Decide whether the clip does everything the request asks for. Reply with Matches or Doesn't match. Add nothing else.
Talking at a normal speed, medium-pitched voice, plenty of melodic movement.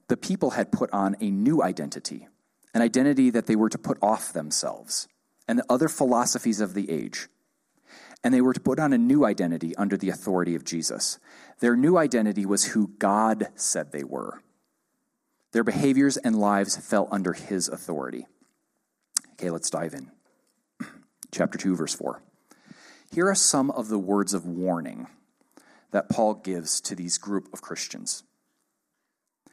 Doesn't match